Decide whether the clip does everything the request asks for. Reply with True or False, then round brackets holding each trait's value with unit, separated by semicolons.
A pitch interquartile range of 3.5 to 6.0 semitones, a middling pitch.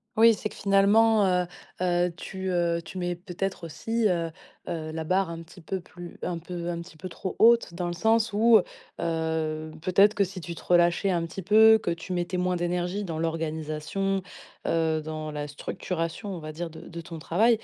False (2.9 semitones; 175 Hz)